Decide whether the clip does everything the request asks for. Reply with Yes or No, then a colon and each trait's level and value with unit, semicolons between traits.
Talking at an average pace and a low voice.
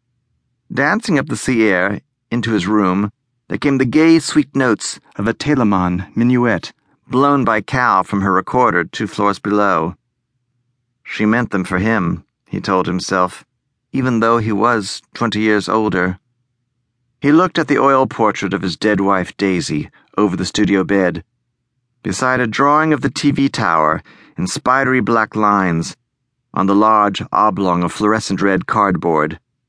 Yes: average, 155 wpm; low, 110 Hz